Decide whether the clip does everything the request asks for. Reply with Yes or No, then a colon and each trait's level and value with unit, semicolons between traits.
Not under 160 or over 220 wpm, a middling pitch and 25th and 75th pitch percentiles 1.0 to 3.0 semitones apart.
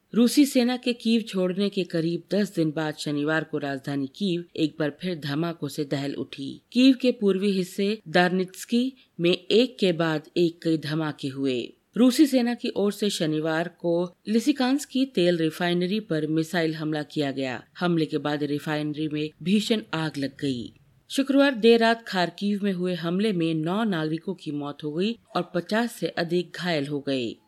No: average, 175 wpm; medium, 175 Hz; average, 5.2 semitones